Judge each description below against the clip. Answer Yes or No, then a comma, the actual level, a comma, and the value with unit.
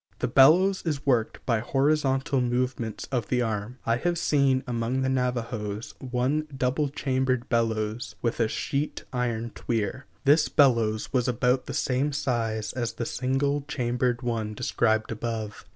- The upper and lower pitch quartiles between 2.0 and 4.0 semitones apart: Yes, average, 2.7 semitones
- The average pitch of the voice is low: Yes, low, 125 Hz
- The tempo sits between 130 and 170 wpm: Yes, average, 150 wpm